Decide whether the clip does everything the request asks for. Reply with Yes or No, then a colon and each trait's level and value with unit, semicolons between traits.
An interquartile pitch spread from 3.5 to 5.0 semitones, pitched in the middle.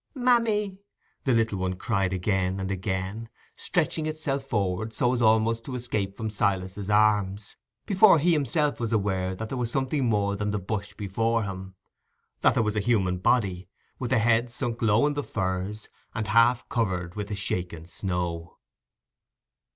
No: average, 4.1 semitones; low, 105 Hz